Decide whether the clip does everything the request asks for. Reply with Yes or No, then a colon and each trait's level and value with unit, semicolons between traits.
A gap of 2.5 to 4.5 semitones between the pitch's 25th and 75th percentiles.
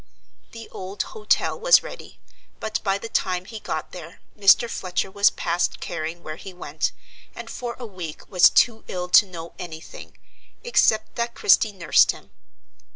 Yes: average, 3.8 semitones